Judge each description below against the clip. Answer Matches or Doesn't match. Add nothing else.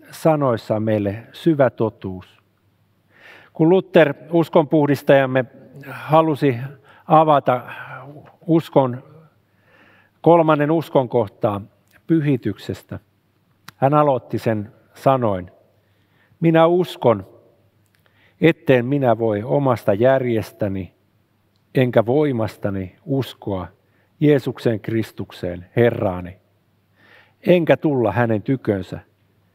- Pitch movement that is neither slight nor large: Doesn't match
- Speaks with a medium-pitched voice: Doesn't match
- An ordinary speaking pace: Doesn't match